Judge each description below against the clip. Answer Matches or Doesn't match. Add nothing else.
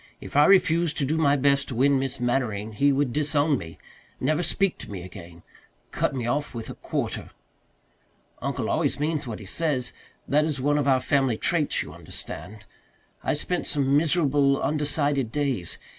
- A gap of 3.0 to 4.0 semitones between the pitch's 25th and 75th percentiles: Matches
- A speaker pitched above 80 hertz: Matches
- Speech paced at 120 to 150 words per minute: Doesn't match